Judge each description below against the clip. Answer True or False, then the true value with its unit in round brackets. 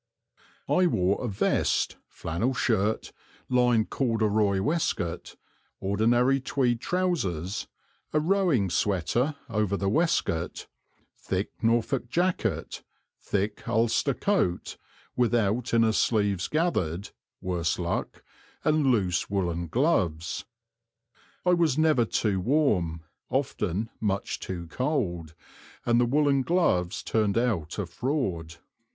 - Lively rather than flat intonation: True (6.4 semitones)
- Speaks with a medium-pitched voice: False (110 Hz)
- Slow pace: True (105 wpm)